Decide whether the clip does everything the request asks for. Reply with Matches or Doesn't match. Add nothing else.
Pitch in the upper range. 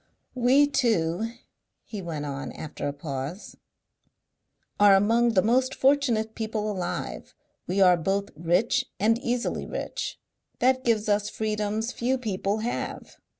Matches